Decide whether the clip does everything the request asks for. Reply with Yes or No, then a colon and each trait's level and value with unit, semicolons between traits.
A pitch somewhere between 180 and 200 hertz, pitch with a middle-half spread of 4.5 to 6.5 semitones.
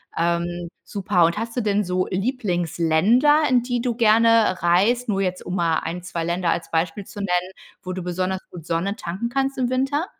Yes: high, 190 Hz; average, 5.2 semitones